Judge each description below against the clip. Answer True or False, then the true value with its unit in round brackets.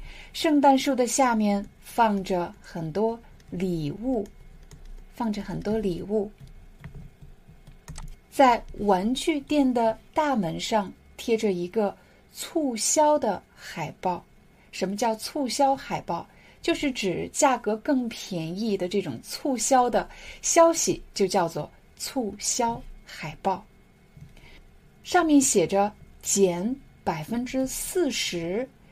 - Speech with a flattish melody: False (5.4 semitones)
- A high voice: True (225 Hz)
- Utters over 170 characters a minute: False (155 characters per minute)